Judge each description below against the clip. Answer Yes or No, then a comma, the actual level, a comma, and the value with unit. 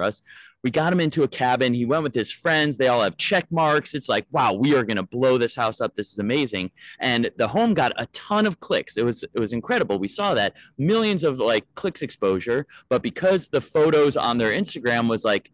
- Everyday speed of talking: No, fast, 235 wpm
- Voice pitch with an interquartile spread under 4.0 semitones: No, average, 5.2 semitones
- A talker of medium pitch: No, low, 130 Hz